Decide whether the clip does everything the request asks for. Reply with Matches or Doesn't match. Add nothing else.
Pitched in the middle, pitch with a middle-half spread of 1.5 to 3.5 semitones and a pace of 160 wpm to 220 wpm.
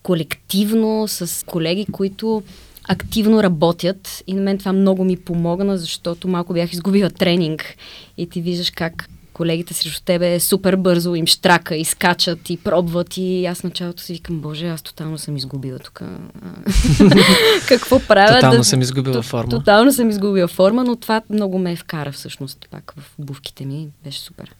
Matches